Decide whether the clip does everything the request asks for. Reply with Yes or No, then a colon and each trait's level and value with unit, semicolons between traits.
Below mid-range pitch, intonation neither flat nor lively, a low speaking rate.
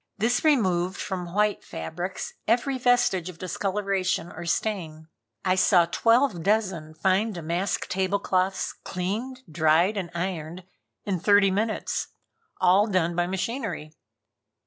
No: medium, 185 Hz; average, 3.2 semitones; slow, 125 wpm